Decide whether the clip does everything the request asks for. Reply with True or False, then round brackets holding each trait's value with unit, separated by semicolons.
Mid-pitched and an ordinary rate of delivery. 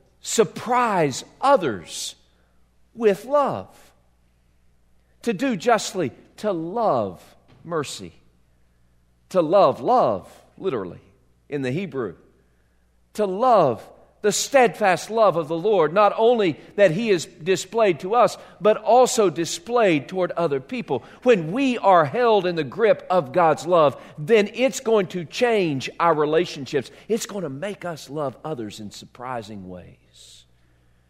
False (170 Hz; 125 wpm)